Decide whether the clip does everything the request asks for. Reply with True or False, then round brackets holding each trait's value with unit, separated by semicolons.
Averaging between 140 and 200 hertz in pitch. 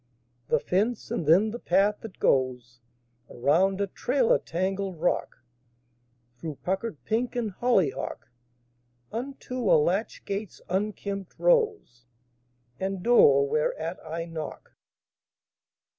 True (190 Hz)